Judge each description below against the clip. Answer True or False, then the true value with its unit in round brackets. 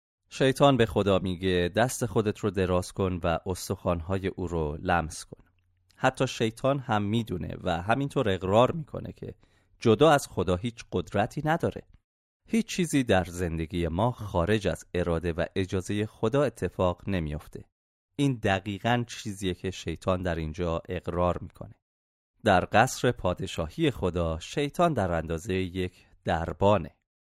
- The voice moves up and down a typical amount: True (4.6 semitones)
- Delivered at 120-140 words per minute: True (135 wpm)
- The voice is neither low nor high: False (95 Hz)